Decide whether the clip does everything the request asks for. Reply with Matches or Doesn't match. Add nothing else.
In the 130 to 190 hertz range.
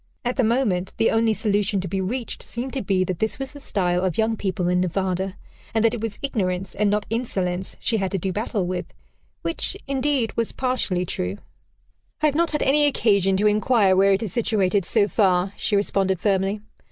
Doesn't match